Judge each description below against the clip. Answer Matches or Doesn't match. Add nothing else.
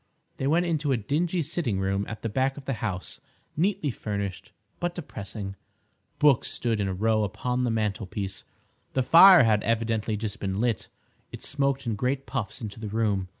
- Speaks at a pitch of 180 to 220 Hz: Doesn't match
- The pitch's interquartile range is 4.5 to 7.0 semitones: Matches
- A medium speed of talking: Matches